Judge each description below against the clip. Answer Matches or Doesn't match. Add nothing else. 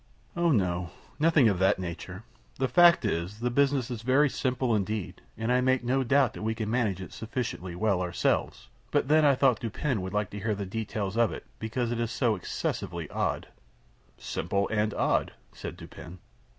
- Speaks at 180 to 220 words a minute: Matches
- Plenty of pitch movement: Doesn't match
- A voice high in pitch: Doesn't match